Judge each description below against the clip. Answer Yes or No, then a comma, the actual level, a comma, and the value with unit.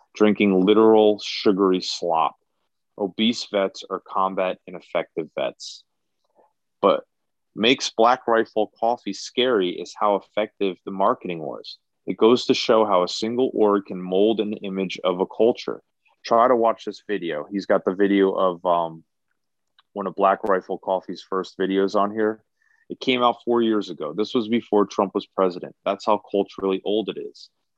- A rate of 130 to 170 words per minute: Yes, average, 160 wpm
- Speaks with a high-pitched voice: No, low, 100 Hz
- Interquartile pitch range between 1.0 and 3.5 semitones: Yes, narrow, 2.6 semitones